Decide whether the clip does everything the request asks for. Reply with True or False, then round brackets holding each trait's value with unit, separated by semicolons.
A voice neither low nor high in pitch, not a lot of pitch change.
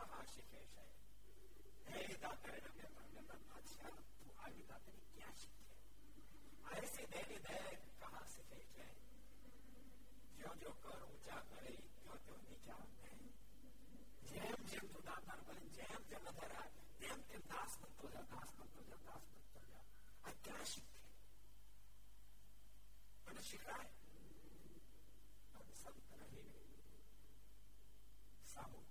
False (105 Hz; 1.2 semitones)